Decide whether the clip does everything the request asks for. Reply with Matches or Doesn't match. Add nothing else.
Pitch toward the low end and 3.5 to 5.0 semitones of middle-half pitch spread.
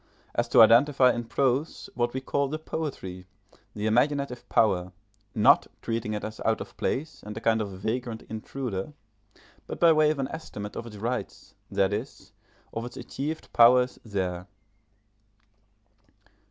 Matches